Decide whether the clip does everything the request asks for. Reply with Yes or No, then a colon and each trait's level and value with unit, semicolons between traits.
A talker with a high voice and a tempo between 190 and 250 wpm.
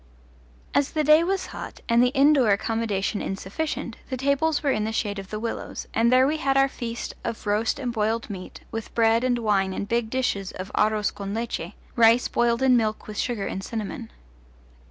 Yes: high, 230 Hz; average, 195 wpm